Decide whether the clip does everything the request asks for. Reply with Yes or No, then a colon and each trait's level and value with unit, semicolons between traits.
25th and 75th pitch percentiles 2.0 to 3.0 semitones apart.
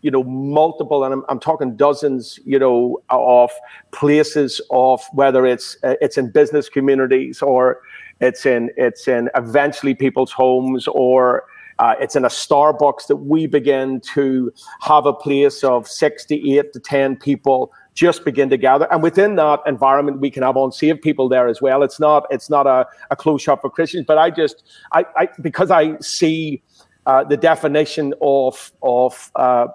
Yes: narrow, 2.5 semitones